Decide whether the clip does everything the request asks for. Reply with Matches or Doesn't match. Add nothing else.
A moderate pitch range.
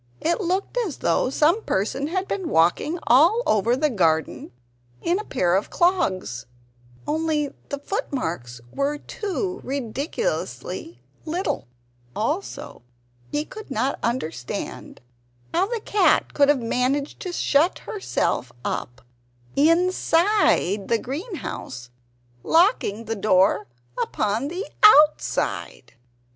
Doesn't match